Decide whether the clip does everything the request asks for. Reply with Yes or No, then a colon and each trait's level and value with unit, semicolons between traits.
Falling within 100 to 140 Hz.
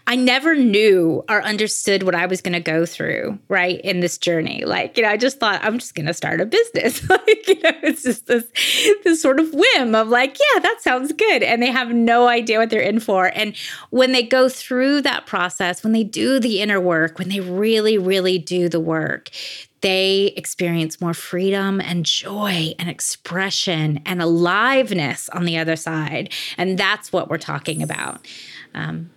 No: high, 205 Hz